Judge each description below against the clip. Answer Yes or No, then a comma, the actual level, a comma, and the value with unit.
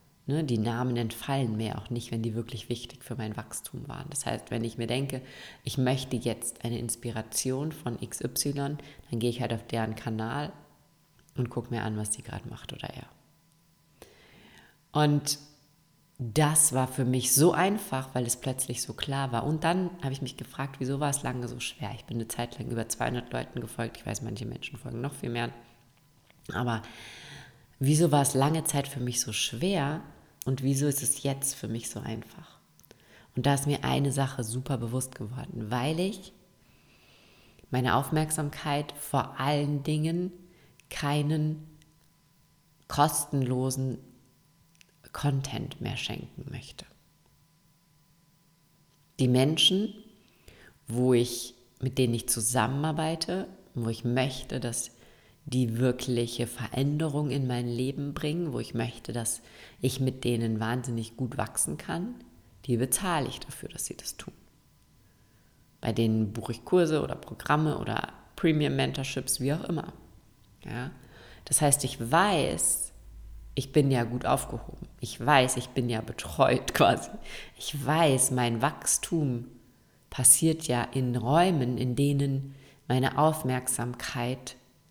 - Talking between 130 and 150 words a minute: Yes, average, 145 wpm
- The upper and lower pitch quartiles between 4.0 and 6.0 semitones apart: No, average, 3.5 semitones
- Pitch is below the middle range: Yes, low, 130 Hz